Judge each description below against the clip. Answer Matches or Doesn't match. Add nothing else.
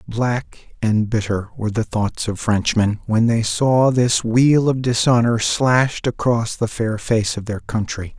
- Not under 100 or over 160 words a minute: Doesn't match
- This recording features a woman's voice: Doesn't match